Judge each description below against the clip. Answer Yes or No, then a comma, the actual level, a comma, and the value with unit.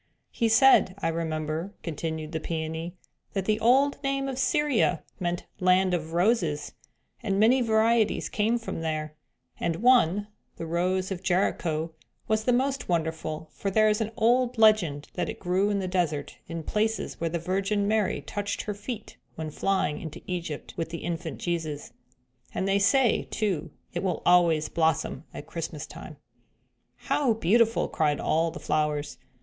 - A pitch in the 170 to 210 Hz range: Yes, medium, 185 Hz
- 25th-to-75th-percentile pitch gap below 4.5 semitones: No, average, 5.1 semitones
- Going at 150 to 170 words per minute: Yes, average, 165 wpm